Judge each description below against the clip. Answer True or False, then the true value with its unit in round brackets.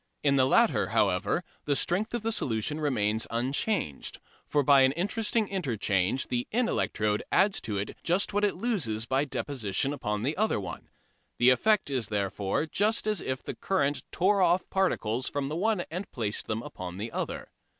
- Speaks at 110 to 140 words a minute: False (180 wpm)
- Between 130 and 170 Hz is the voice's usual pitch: True (140 Hz)